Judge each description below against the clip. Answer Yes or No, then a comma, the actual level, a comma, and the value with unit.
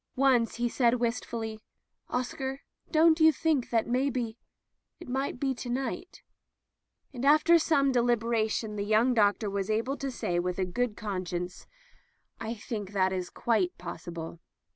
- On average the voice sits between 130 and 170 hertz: No, high, 235 Hz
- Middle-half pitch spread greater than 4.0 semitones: Yes, average, 4.4 semitones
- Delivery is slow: No, average, 160 wpm